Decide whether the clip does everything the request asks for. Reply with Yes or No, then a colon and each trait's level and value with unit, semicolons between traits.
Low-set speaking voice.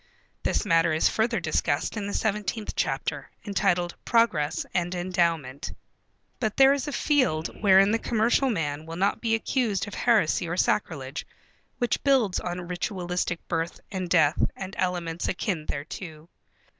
No: medium, 180 Hz